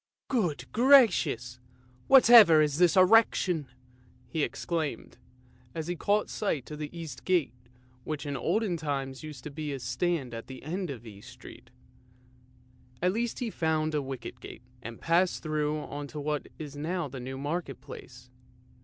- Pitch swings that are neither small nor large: Yes, average, 4.7 semitones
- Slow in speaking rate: No, average, 160 wpm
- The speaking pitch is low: No, medium, 150 Hz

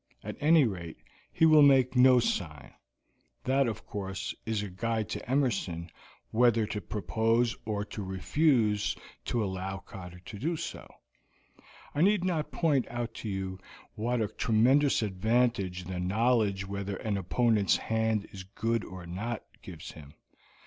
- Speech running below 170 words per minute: Yes, average, 150 wpm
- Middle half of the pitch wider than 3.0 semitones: Yes, average, 4.3 semitones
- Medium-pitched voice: No, low, 110 Hz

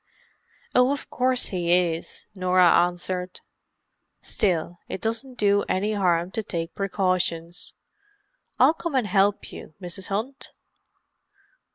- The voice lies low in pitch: No, medium, 185 Hz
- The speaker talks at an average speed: No, slow, 115 wpm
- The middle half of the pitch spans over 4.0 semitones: No, average, 3.5 semitones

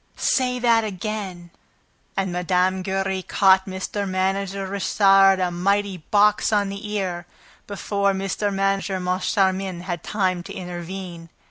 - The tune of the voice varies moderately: No, narrow, 1.5 semitones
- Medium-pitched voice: No, high, 195 Hz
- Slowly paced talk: Yes, slow, 125 wpm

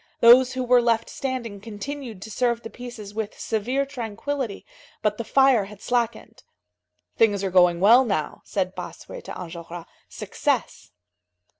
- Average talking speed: Yes, average, 145 wpm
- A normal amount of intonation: Yes, average, 3.7 semitones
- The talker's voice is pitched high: Yes, high, 225 Hz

